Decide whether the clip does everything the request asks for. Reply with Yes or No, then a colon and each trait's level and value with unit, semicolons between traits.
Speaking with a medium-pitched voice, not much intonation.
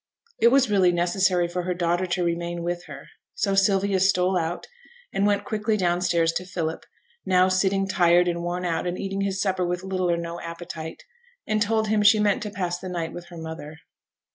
Yes: medium, 180 Hz; narrow, 2.1 semitones